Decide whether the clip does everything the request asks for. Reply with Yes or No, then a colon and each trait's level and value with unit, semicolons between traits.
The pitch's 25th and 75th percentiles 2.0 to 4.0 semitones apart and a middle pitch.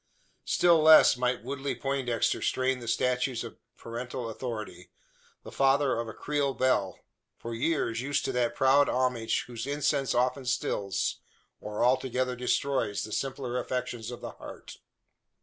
No: narrow, 2.5 semitones; low, 125 Hz